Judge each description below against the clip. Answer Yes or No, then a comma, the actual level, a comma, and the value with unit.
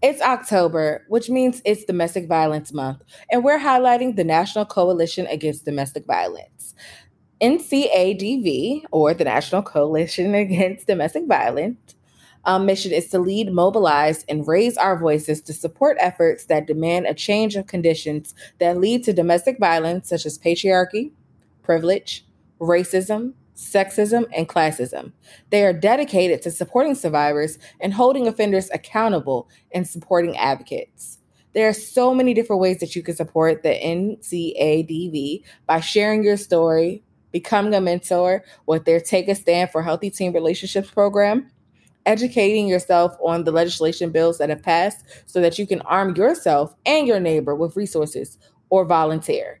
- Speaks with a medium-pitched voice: Yes, medium, 180 Hz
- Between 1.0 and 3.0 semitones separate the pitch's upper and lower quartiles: No, average, 4.3 semitones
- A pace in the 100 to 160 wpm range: Yes, average, 145 wpm